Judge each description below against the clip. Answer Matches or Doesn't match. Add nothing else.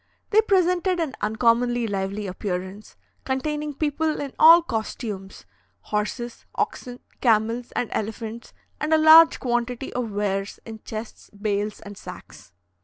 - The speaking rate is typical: Doesn't match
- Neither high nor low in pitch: Doesn't match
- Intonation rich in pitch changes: Matches